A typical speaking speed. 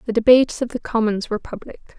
No: fast, 210 wpm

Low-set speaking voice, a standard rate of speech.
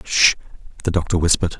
Yes: very low, 85 Hz; average, 150 wpm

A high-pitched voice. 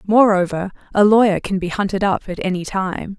Yes: high, 195 Hz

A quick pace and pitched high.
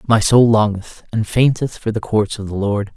No: fast, 225 wpm; low, 110 Hz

